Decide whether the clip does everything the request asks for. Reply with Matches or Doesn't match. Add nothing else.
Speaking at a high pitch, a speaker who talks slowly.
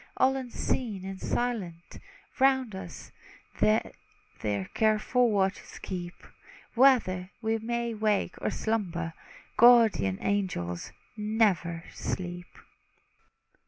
Matches